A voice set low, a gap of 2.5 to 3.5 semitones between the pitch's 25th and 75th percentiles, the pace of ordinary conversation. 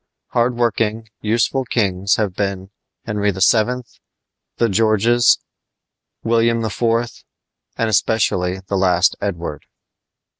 No: low, 110 Hz; average, 3.2 semitones; slow, 100 wpm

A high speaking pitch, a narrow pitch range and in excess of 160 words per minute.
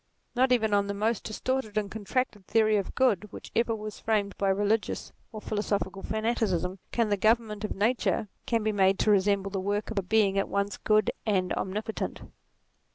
Yes: high, 210 Hz; narrow, 1.8 semitones; average, 180 wpm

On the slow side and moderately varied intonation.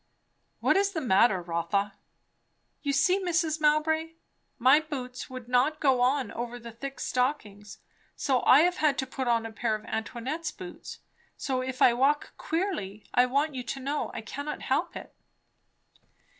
No: average, 165 wpm; average, 4.3 semitones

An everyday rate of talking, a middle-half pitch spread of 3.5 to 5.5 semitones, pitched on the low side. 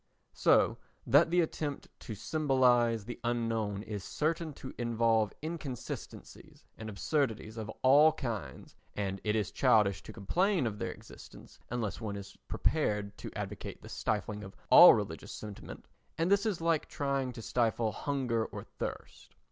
Yes: average, 150 wpm; average, 5.2 semitones; low, 115 Hz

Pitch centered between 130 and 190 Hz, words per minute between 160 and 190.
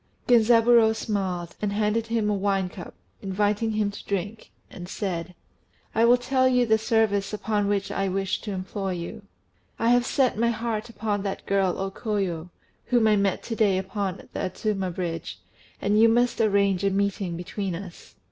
No: high, 205 Hz; average, 175 wpm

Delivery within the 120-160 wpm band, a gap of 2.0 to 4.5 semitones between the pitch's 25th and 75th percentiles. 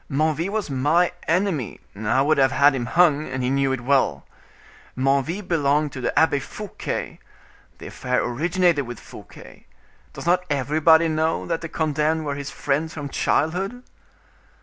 Yes: average, 150 wpm; average, 3.4 semitones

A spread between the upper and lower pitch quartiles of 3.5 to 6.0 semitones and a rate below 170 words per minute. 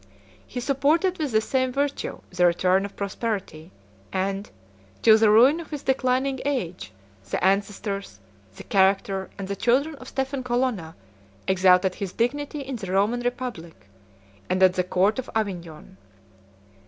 Yes: wide, 5.5 semitones; average, 145 wpm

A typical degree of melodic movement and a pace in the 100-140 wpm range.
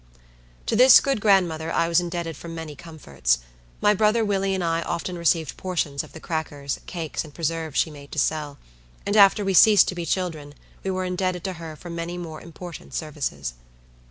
No: average, 3.0 semitones; average, 190 wpm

